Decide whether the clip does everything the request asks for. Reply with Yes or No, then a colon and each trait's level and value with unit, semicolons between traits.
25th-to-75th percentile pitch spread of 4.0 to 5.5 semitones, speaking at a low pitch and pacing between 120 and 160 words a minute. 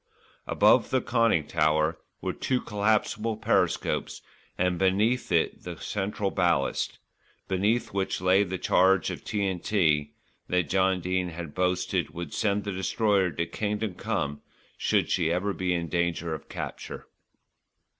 No: average, 3.0 semitones; very low, 95 Hz; slow, 135 wpm